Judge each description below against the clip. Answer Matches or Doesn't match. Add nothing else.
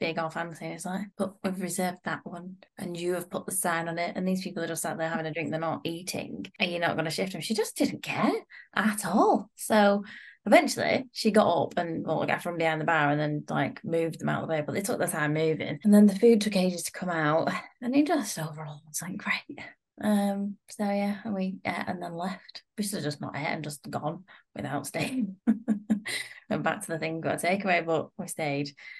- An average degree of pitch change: Matches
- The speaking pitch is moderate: Matches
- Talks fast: Matches